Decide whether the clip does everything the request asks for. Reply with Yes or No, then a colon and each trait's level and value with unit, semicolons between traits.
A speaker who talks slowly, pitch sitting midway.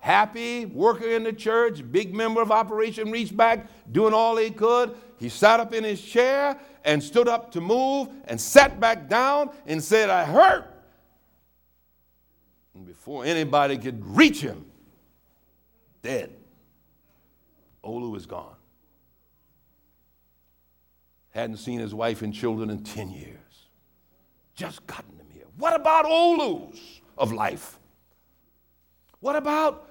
Yes: slow, 130 wpm; medium, 165 Hz